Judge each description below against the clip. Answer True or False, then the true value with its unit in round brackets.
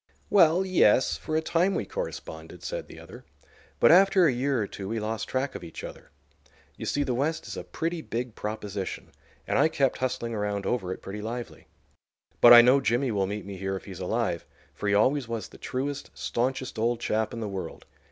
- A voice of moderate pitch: False (120 Hz)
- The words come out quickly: True (210 wpm)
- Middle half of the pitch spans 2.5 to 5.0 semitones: False (5.4 semitones)